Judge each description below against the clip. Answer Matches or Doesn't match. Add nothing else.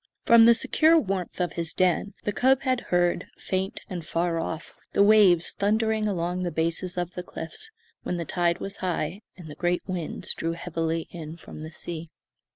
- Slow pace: Doesn't match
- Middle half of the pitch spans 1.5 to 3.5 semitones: Matches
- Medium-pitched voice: Matches